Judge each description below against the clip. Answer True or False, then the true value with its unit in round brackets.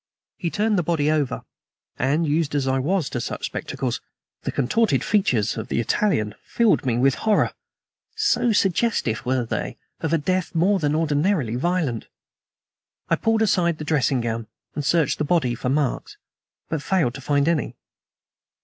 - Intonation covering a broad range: True (6.0 semitones)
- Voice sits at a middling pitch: True (150 Hz)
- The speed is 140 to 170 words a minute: True (165 wpm)